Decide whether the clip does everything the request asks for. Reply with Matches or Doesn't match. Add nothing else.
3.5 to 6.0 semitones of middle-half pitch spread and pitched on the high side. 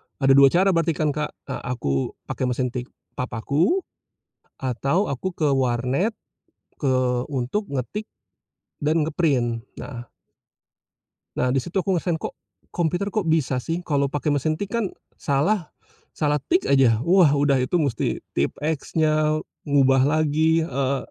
Doesn't match